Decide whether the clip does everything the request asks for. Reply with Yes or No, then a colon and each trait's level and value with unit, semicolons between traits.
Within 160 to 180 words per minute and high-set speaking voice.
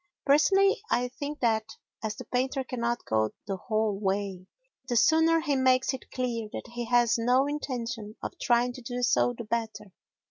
Yes: average, 175 wpm; high, 240 Hz